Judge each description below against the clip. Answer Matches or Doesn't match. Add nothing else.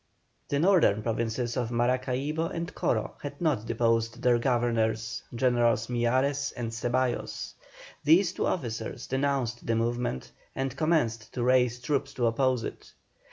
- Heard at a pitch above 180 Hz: Doesn't match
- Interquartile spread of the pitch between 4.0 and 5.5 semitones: Doesn't match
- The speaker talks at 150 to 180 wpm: Doesn't match